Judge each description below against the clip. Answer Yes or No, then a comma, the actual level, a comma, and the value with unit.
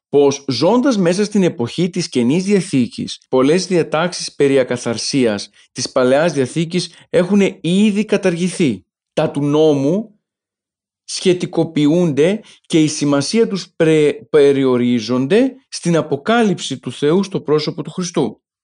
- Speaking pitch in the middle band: Yes, medium, 165 Hz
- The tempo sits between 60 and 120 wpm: Yes, slow, 115 wpm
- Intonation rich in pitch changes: No, average, 4.9 semitones